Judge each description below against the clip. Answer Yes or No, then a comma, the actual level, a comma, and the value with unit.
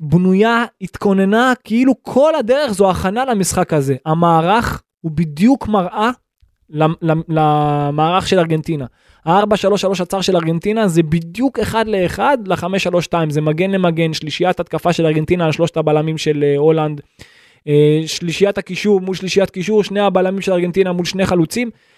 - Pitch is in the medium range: Yes, medium, 180 Hz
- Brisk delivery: No, average, 135 wpm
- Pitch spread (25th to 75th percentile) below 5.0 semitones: Yes, average, 4.0 semitones